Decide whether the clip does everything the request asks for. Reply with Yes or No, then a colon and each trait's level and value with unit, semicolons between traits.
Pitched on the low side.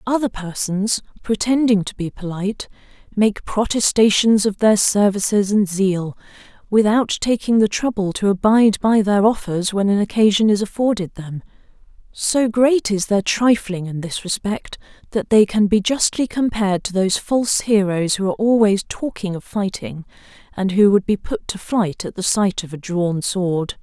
No: high, 205 Hz